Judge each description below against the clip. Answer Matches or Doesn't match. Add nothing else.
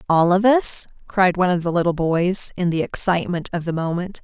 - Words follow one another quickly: Matches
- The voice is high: Doesn't match